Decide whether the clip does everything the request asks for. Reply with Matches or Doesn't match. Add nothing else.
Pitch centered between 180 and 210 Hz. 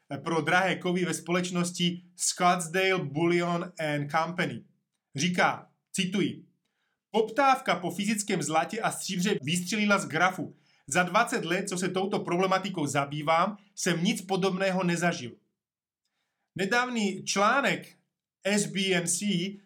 Matches